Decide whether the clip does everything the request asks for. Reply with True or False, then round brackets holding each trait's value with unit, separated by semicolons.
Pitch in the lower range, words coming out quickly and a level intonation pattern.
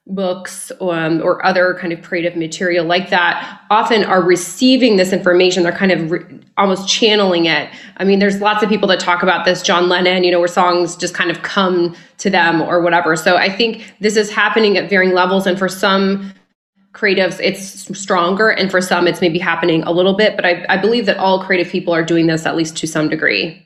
False (185 Hz; 220 wpm; 2.1 semitones)